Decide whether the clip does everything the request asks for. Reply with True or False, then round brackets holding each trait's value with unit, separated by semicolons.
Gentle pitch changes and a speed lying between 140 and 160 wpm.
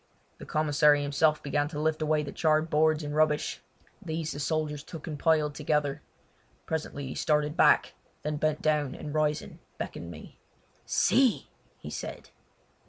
True (1.1 semitones; 155 wpm)